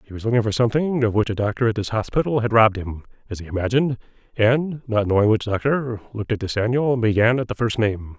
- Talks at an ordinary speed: No, fast, 240 wpm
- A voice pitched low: Yes, low, 115 Hz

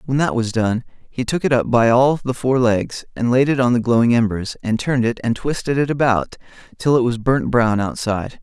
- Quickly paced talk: Yes, fast, 235 wpm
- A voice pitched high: No, low, 120 Hz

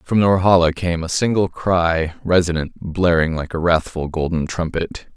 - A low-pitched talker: Yes, very low, 85 Hz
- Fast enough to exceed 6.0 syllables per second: No, 4.5 syllables/s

